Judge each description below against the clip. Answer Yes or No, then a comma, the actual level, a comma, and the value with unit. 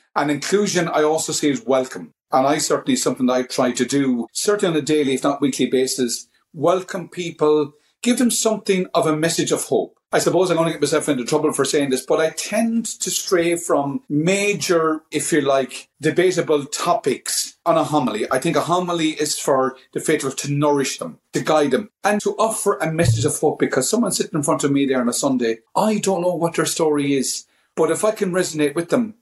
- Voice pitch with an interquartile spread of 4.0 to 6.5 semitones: Yes, average, 4.5 semitones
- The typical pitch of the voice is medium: Yes, medium, 155 Hz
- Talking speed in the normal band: No, fast, 220 wpm